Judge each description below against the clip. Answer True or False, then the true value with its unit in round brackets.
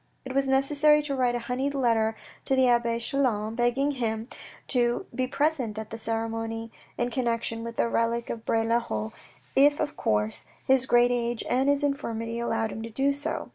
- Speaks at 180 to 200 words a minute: True (190 wpm)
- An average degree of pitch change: True (3.1 semitones)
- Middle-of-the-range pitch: False (240 Hz)